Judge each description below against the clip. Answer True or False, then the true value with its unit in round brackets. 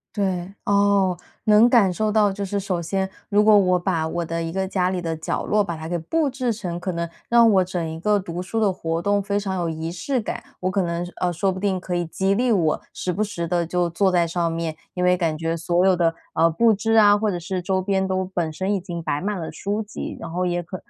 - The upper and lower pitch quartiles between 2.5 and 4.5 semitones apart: True (3.0 semitones)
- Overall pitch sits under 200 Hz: True (185 Hz)